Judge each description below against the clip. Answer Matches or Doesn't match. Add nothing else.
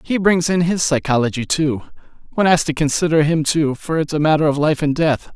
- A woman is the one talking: Doesn't match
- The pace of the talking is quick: Matches